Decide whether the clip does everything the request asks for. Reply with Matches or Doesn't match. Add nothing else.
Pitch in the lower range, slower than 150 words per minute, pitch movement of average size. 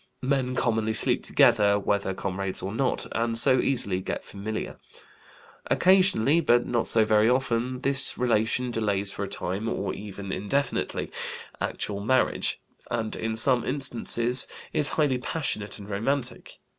Matches